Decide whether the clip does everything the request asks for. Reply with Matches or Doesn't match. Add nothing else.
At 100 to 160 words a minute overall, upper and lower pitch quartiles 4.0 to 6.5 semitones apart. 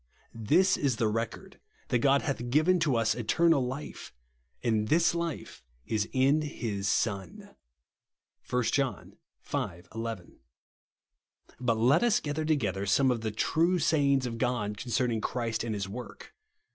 Matches